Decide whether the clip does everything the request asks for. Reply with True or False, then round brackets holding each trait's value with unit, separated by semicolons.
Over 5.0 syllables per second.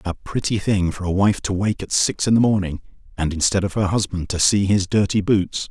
True (5.3 syllables/s)